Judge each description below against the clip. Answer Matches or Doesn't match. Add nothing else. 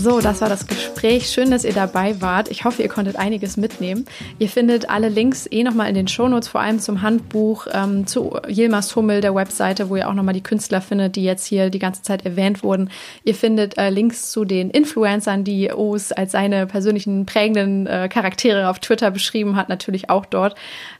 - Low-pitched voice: Doesn't match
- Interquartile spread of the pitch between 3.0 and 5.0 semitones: Doesn't match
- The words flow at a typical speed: Doesn't match